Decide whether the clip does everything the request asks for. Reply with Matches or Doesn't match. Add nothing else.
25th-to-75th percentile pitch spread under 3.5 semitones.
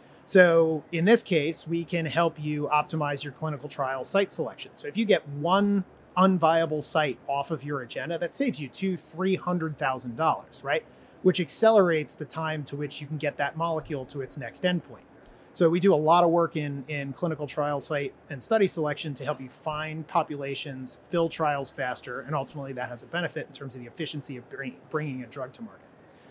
Matches